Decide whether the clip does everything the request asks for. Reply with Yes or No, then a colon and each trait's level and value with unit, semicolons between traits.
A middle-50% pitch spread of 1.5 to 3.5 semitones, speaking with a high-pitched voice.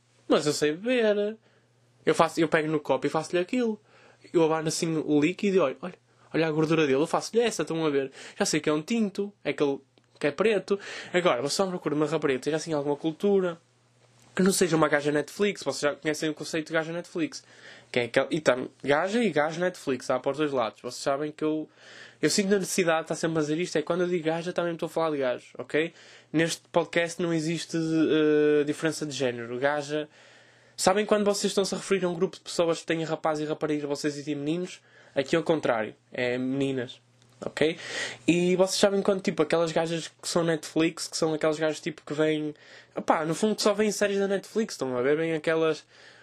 No: average, 3.2 semitones; medium, 160 Hz